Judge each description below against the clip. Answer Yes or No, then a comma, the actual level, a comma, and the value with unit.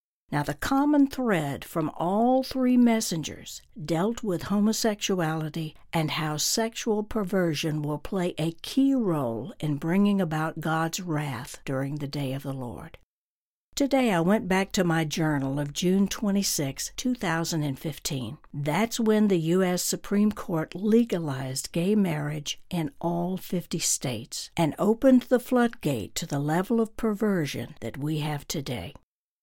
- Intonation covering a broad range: Yes, wide, 5.9 semitones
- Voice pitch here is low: No, medium, 170 Hz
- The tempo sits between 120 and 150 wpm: Yes, average, 140 wpm